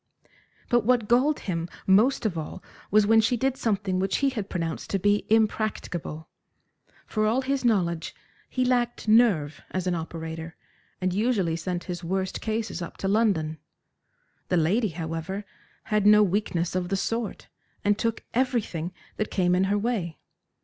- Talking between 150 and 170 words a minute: Yes, average, 160 wpm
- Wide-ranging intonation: No, average, 4.5 semitones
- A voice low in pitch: No, high, 200 Hz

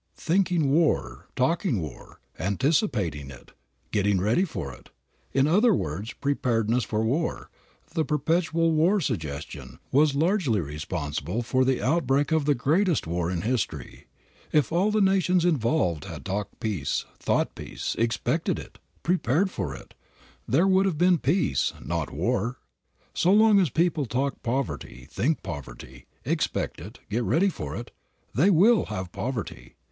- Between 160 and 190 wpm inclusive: No, average, 145 wpm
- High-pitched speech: No, low, 130 Hz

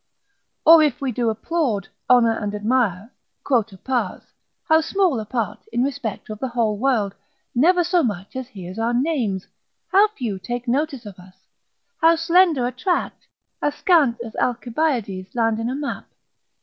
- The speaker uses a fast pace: No, average, 160 wpm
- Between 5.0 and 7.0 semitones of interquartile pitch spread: Yes, wide, 5.5 semitones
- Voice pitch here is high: Yes, high, 245 Hz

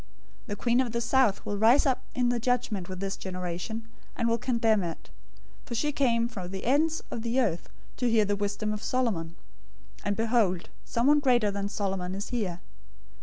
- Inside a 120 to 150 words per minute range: No, average, 190 wpm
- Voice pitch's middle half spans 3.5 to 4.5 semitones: Yes, average, 3.8 semitones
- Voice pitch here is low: No, high, 225 Hz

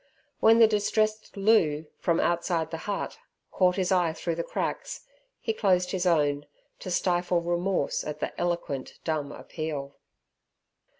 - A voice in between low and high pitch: Yes, medium, 175 Hz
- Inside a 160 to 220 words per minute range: No, average, 140 wpm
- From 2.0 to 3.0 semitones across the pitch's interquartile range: No, average, 3.5 semitones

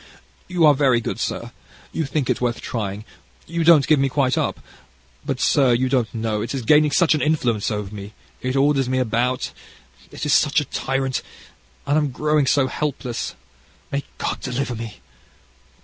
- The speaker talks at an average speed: Yes, average, 180 wpm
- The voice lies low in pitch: Yes, low, 130 Hz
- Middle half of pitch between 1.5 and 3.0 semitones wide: No, average, 3.8 semitones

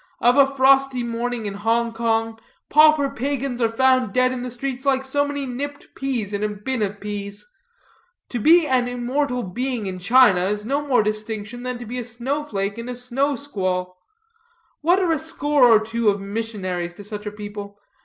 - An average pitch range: Yes, average, 4.3 semitones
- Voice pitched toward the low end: No, high, 240 Hz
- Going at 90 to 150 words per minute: No, average, 195 wpm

